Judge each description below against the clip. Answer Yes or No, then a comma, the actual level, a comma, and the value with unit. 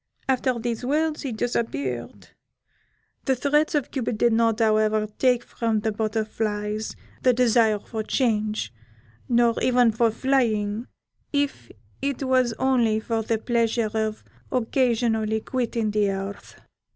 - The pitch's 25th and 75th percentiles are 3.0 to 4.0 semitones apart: No, narrow, 2.6 semitones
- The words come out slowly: Yes, slow, 125 wpm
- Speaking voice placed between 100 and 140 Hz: No, high, 230 Hz